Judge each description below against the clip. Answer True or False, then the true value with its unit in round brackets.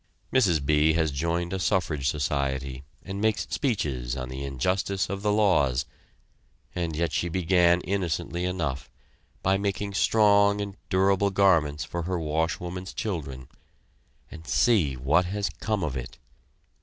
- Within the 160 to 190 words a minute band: False (140 wpm)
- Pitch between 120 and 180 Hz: False (85 Hz)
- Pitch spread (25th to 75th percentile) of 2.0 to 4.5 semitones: False (4.9 semitones)